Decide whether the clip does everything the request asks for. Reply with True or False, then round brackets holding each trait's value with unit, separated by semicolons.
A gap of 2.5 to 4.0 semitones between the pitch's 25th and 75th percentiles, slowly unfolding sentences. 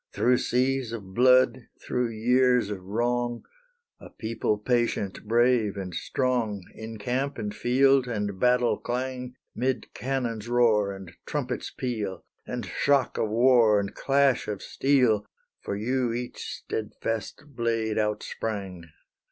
True (3.1 semitones; 130 wpm)